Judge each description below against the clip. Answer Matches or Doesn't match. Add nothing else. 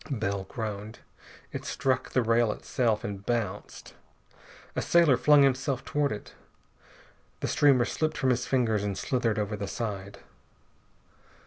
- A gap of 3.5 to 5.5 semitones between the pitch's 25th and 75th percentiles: Matches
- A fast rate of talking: Doesn't match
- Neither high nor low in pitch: Doesn't match